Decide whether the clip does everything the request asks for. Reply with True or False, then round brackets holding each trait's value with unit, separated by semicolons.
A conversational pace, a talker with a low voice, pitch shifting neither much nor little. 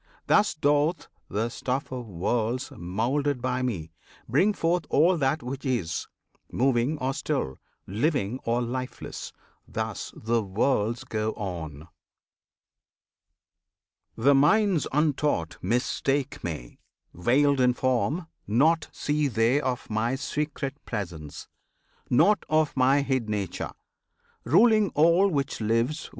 False (115 wpm; 130 Hz; 4.7 semitones)